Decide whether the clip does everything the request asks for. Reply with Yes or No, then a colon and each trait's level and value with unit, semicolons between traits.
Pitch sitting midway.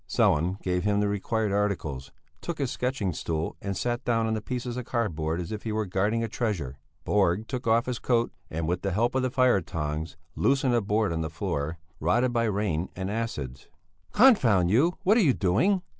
No: low, 105 Hz